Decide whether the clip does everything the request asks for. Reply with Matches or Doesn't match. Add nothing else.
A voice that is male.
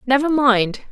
Doesn't match